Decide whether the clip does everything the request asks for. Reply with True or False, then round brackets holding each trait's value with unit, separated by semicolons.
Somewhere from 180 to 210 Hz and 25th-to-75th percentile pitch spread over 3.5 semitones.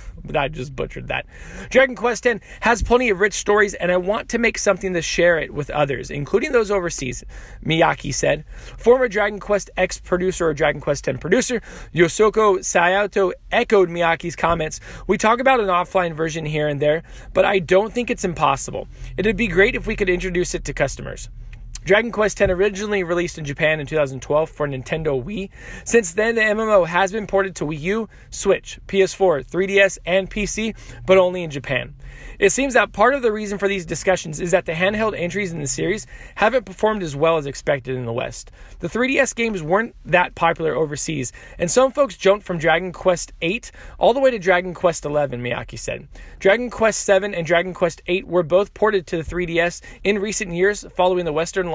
True (185 Hz; 4.4 semitones)